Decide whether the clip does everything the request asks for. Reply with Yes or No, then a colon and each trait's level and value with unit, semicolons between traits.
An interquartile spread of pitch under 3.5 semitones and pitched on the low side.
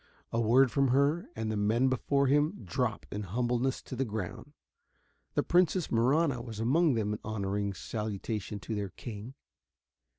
No: average, 4.3 semitones; low, 120 Hz